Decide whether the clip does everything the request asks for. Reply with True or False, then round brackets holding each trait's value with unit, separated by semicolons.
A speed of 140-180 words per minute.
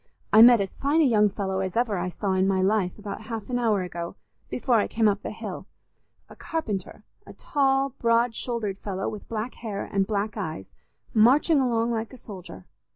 False (195 wpm)